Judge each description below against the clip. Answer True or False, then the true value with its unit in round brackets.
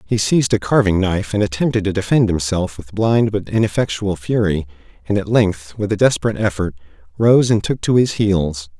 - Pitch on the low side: True (100 Hz)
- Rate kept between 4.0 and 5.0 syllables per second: False (5.5 syllables/s)